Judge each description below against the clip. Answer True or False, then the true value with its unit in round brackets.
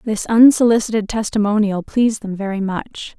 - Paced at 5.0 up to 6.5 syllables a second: True (5.3 syllables/s)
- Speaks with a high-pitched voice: True (210 Hz)